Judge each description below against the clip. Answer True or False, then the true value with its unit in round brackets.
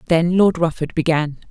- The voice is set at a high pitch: False (165 Hz)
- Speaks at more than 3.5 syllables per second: True (4.7 syllables/s)